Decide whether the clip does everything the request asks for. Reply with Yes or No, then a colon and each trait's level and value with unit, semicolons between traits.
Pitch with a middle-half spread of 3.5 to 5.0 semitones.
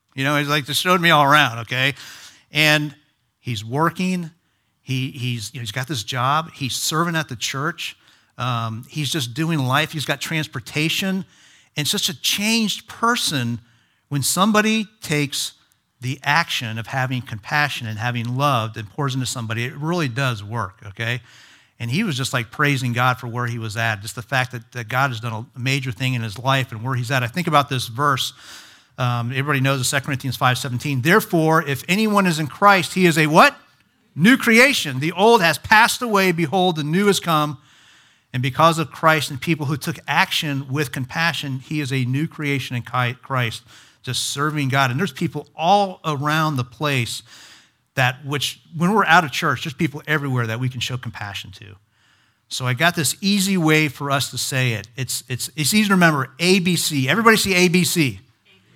Yes: average, 4.7 semitones